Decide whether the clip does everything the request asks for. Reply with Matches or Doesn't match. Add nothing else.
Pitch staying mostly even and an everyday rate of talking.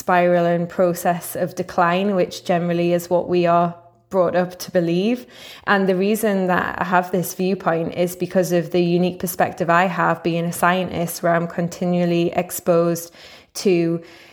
Matches